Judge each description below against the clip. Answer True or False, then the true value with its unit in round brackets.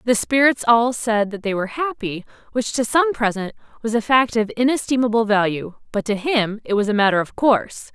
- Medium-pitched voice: False (230 Hz)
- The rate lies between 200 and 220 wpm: True (205 wpm)